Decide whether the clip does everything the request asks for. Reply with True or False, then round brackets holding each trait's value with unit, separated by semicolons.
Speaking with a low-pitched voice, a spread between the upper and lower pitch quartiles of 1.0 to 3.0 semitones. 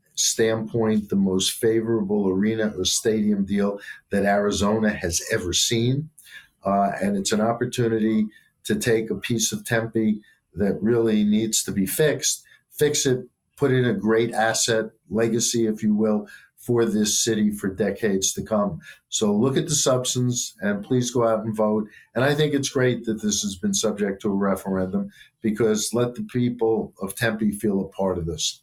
True (110 Hz; 2.7 semitones)